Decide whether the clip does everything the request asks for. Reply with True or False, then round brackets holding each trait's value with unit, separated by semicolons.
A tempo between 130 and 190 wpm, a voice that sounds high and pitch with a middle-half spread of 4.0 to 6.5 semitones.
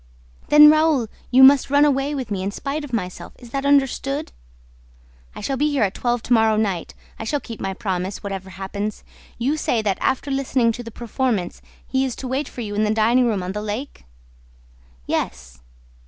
False (200 wpm; 235 Hz; 5.0 semitones)